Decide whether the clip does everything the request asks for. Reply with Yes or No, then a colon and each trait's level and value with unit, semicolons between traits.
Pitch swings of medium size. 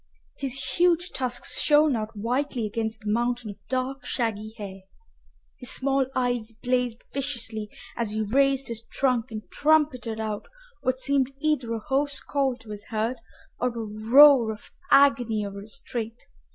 Yes: average, 3.8 semitones